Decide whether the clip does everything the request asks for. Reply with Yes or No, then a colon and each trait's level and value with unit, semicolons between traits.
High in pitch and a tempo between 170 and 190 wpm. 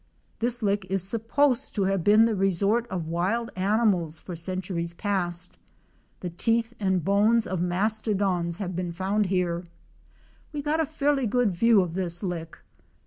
No: high, 195 Hz; average, 155 wpm